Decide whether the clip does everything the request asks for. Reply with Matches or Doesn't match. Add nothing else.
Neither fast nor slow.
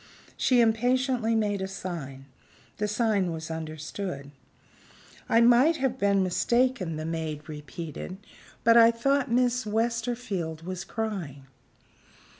Doesn't match